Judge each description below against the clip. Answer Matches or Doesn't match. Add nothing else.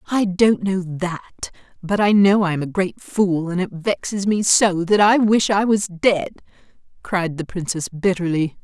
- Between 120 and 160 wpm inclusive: Doesn't match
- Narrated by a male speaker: Doesn't match